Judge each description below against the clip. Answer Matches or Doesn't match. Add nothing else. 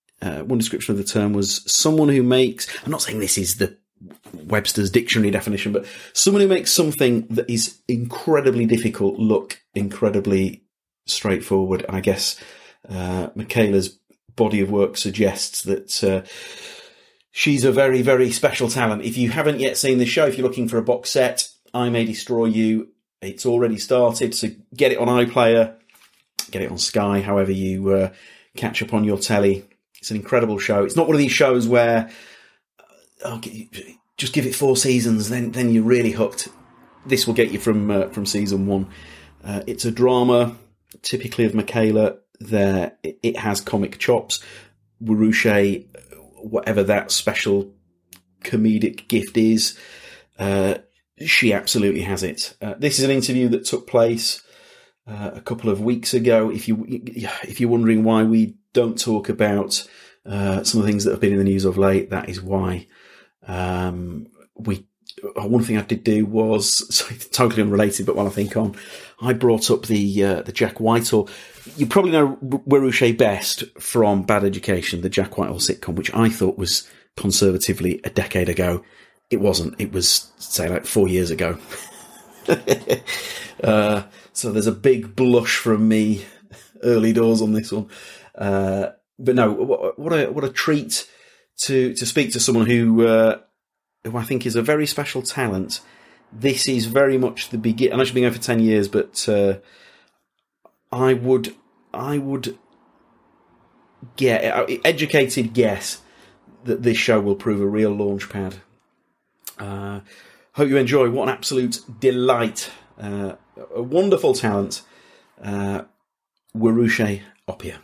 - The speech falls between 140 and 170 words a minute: Matches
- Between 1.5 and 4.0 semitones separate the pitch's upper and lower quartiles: Matches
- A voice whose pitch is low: Matches